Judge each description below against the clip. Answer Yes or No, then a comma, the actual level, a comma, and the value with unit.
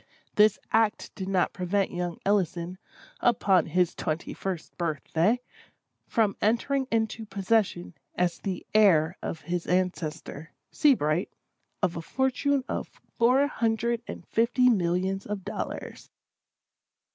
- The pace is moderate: No, slow, 120 wpm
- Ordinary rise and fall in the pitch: Yes, average, 4.4 semitones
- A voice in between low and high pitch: No, high, 195 Hz